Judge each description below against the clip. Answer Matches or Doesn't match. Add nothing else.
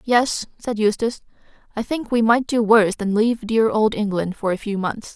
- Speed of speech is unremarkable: Doesn't match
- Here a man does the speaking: Doesn't match